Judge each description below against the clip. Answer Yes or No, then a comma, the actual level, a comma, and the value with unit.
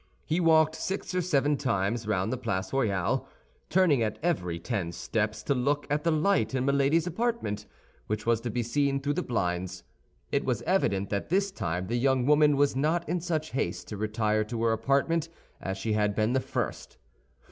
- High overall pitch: No, low, 125 Hz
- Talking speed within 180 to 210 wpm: Yes, average, 190 wpm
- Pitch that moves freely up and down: Yes, wide, 6.3 semitones